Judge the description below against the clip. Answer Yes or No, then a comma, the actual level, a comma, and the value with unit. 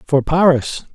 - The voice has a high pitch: No, medium, 150 Hz